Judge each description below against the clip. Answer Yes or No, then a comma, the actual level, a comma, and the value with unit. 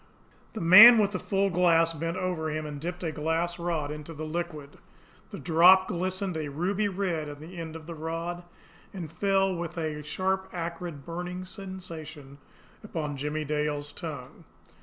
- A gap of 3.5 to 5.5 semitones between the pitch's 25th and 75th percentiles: No, average, 3.0 semitones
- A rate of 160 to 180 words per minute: Yes, average, 165 wpm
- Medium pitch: Yes, medium, 170 Hz